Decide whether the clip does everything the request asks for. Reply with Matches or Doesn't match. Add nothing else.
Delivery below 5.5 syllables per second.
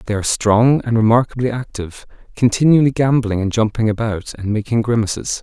Doesn't match